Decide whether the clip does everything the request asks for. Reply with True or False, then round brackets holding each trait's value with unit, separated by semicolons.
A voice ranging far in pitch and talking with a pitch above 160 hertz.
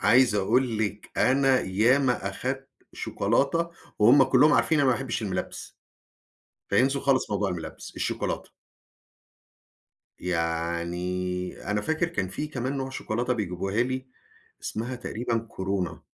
False (5.7 semitones; 115 Hz)